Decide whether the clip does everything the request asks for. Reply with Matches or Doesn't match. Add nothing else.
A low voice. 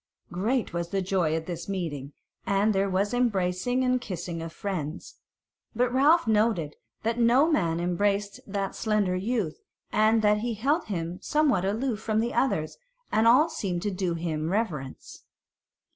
Doesn't match